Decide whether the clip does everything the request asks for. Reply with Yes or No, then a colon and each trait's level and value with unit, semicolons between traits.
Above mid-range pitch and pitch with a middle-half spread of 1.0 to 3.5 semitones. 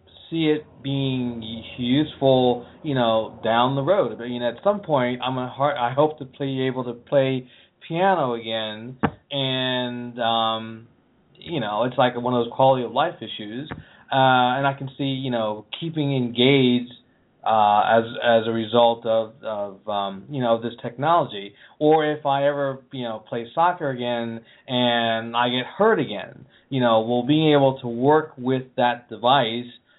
No: low, 125 Hz; average, 3.0 semitones